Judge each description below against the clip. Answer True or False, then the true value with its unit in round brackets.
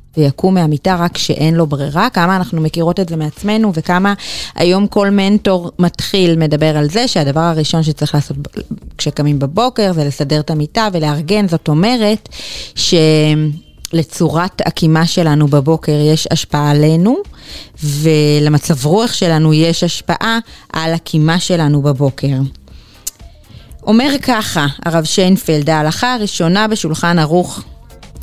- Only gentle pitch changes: False (3.7 semitones)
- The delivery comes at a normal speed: True (120 wpm)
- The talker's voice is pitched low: False (165 Hz)